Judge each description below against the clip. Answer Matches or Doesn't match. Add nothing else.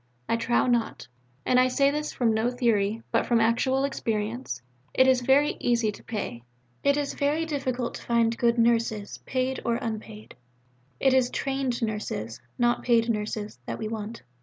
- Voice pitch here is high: Matches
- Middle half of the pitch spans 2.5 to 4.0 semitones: Matches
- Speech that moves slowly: Doesn't match